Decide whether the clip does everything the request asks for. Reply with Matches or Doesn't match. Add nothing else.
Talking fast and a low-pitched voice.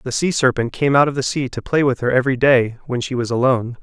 Matches